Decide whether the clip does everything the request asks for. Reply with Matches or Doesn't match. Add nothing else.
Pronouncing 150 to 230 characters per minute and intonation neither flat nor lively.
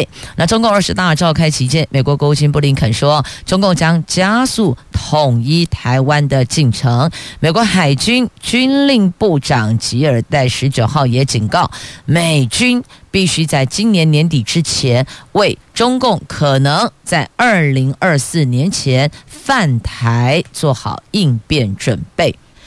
Matches